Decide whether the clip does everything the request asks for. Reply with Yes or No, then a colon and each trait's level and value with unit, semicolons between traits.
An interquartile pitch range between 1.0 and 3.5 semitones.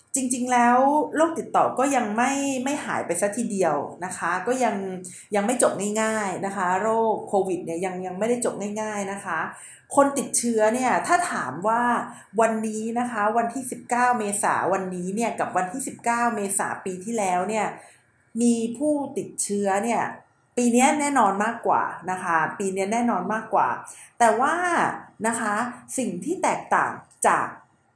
No: average, 4.0 semitones